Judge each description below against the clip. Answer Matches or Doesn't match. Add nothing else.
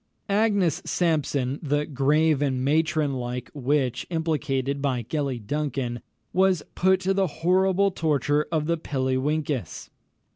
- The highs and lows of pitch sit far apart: Doesn't match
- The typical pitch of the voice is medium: Matches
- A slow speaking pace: Matches